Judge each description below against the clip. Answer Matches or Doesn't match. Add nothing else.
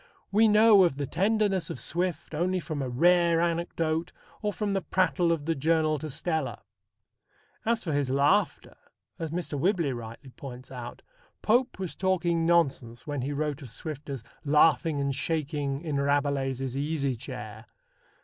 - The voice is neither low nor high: Matches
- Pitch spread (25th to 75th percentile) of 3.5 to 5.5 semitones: Matches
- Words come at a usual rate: Matches